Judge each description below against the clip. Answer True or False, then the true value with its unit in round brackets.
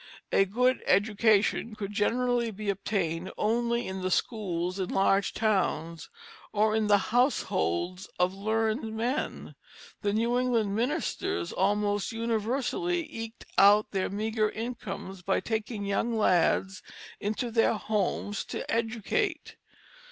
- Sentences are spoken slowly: True (120 wpm)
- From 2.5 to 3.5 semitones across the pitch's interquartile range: True (2.9 semitones)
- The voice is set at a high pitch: True (215 Hz)